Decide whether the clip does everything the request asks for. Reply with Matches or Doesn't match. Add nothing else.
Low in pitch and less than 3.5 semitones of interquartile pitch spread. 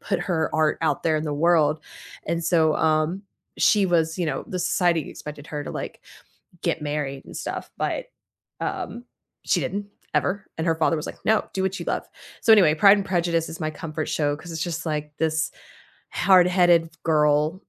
Doesn't match